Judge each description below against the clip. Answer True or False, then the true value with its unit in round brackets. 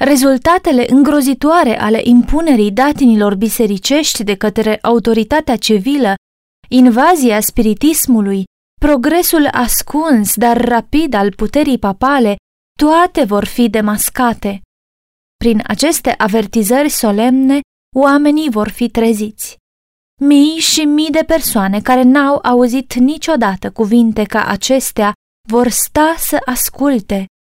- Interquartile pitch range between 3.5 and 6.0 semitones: True (4.9 semitones)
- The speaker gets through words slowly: True (100 wpm)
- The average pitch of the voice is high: True (245 Hz)